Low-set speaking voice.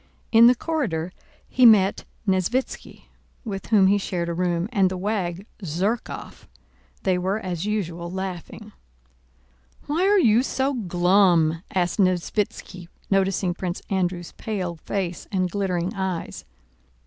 No: high, 190 Hz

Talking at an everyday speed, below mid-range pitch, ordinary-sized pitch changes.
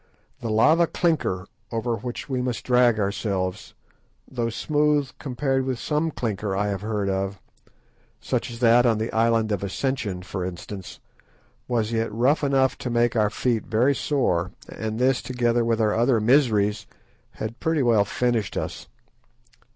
Yes: average, 155 wpm; low, 115 Hz; average, 3.5 semitones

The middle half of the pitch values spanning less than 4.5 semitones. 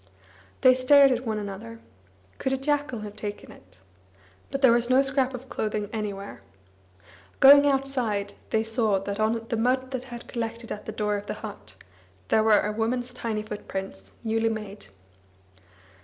Yes: average, 3.5 semitones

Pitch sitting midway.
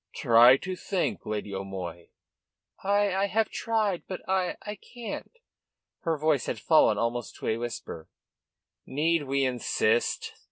Yes: medium, 145 Hz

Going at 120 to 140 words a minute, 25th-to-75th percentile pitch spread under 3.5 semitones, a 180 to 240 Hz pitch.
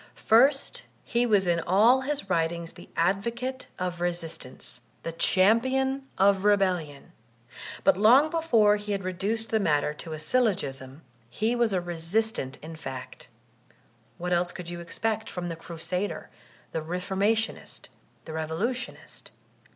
No: slow, 135 wpm; average, 5.1 semitones; high, 190 Hz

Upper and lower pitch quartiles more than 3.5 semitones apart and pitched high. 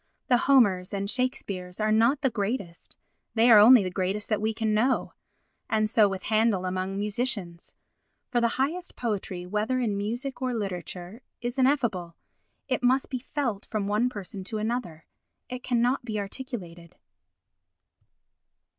Yes: average, 4.1 semitones; high, 215 Hz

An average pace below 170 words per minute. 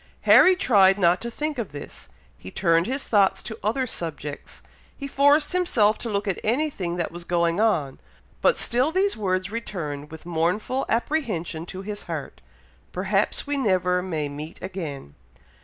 Yes: average, 160 wpm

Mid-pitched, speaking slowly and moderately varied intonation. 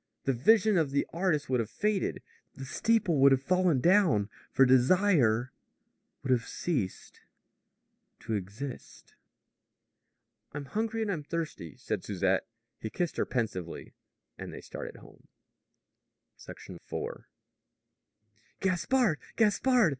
No: medium, 145 Hz; slow, 115 wpm; wide, 7.9 semitones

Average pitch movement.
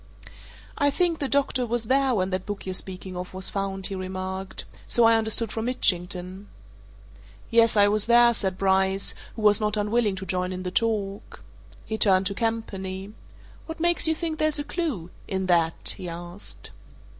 Yes: average, 3.8 semitones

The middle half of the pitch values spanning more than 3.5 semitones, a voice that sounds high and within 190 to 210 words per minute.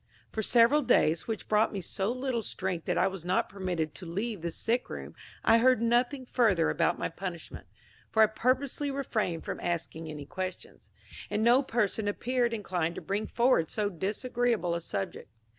No: average, 5.1 semitones; high, 210 Hz; average, 175 wpm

